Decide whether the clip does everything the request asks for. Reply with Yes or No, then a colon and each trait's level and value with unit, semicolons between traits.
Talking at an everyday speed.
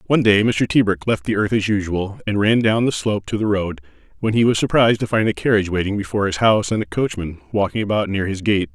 No: fast, 255 wpm